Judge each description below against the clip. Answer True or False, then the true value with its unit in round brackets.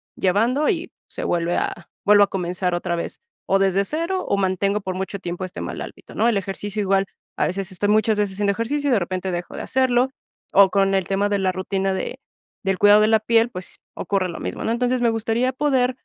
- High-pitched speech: True (200 Hz)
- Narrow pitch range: False (3.5 semitones)